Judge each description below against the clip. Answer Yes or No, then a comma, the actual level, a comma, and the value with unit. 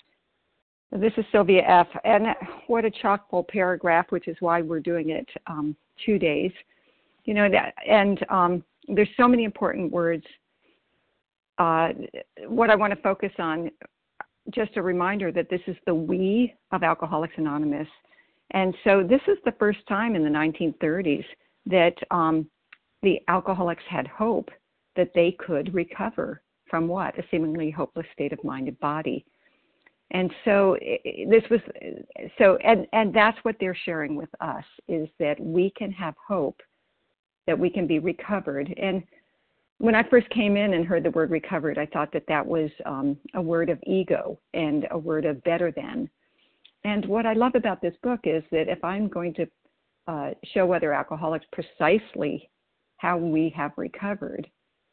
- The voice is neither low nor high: Yes, medium, 180 Hz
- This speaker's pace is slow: No, average, 165 wpm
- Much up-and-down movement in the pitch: No, average, 4.5 semitones